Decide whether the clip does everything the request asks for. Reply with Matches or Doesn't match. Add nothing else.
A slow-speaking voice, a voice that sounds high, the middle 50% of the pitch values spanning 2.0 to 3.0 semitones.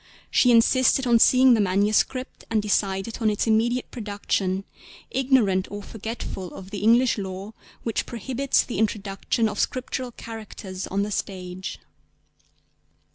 Doesn't match